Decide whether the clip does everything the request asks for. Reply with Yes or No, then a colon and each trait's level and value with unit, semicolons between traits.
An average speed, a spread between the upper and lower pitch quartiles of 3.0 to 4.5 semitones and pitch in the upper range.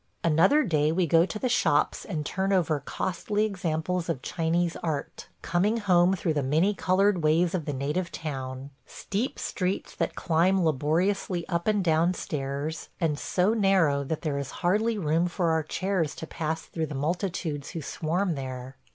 No: average, 175 wpm; average, 3.5 semitones; medium, 170 Hz